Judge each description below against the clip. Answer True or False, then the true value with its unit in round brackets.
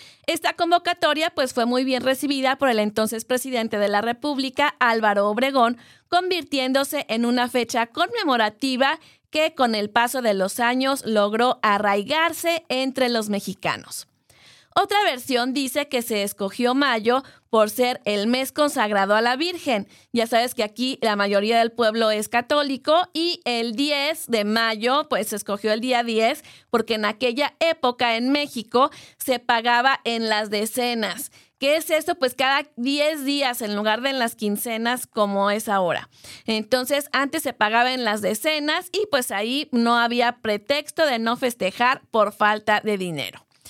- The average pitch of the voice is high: True (245 Hz)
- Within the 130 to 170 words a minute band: True (160 wpm)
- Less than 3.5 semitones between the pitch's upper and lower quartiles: False (4.2 semitones)